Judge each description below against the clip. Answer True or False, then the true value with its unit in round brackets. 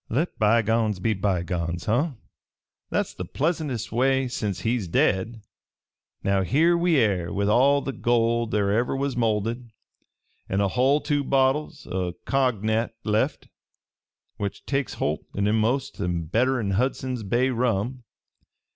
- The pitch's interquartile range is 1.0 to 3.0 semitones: False (4.7 semitones)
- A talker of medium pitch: False (115 Hz)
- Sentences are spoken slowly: True (130 wpm)